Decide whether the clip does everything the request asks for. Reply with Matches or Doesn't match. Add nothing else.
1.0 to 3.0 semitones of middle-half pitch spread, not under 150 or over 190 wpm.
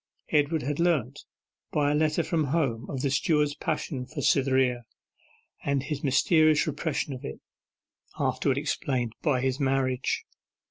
Doesn't match